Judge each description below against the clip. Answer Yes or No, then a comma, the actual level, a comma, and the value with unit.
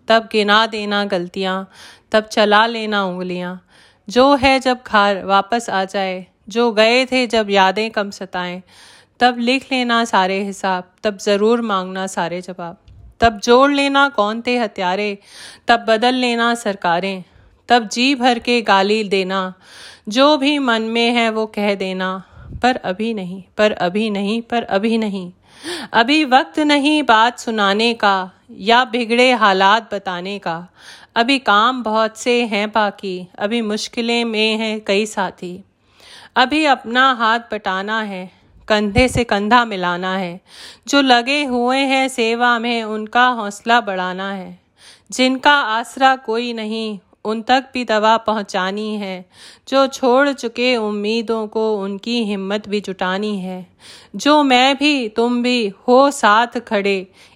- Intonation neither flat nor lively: Yes, average, 3.6 semitones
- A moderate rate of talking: Yes, average, 145 wpm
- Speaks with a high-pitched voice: Yes, high, 220 Hz